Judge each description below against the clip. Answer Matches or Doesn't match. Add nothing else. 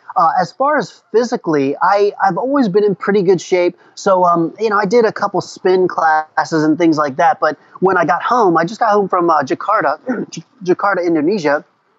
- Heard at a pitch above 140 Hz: Matches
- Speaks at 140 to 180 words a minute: Doesn't match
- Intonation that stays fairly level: Doesn't match